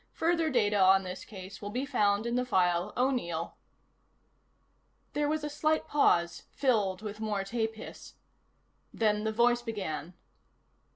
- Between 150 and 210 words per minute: No, average, 140 wpm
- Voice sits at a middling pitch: No, high, 215 Hz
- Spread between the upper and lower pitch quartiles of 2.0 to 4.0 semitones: No, average, 4.5 semitones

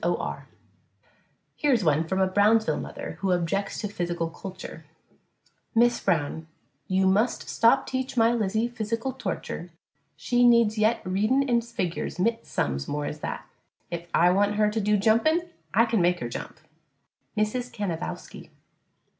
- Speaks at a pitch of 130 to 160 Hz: No, high, 210 Hz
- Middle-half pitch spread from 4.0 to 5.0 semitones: Yes, average, 4.6 semitones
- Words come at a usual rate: Yes, average, 150 wpm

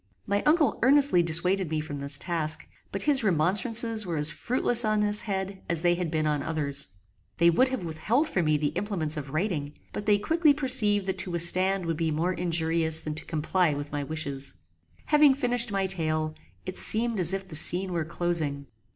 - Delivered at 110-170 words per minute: No, average, 195 wpm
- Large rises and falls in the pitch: No, average, 5.0 semitones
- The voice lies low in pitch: No, medium, 175 Hz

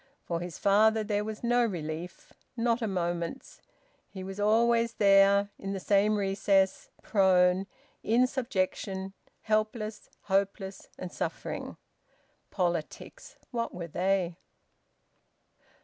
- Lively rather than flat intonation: No, average, 2.7 semitones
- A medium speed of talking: No, slow, 110 wpm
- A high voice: Yes, high, 195 Hz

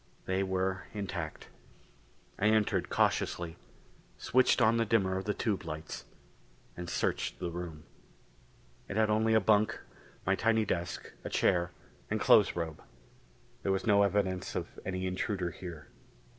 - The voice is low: Yes, very low, 95 Hz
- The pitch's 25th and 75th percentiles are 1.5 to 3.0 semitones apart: No, average, 3.4 semitones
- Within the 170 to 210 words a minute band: No, average, 145 wpm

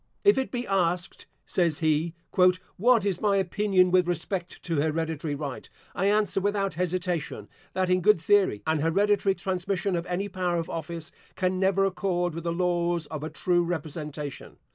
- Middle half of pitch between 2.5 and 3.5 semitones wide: Yes, average, 2.9 semitones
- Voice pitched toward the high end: No, medium, 180 Hz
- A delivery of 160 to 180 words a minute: Yes, average, 165 wpm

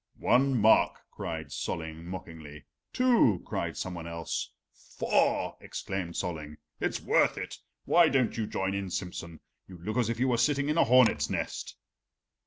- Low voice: Yes, very low, 95 Hz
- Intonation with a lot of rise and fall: Yes, wide, 6.8 semitones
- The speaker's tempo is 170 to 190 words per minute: No, average, 155 wpm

